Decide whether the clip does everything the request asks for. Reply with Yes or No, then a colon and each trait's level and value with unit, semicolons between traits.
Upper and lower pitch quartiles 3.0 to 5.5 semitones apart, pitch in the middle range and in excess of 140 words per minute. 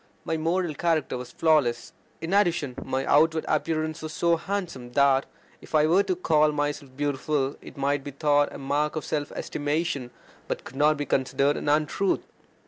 No: narrow, 2.5 semitones; medium, 150 Hz; average, 175 wpm